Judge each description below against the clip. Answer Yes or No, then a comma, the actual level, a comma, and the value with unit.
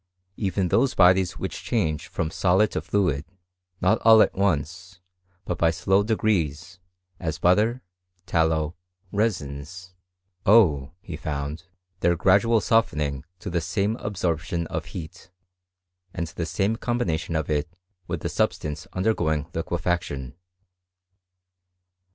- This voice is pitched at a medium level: No, very low, 90 Hz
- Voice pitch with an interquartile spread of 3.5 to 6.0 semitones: Yes, average, 4.1 semitones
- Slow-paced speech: Yes, slow, 120 wpm